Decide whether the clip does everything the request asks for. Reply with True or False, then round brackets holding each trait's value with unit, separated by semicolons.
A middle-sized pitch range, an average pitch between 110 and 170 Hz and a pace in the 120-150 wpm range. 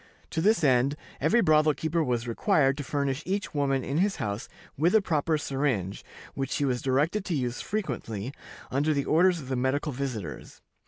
False (3.9 semitones; 140 Hz; 180 wpm)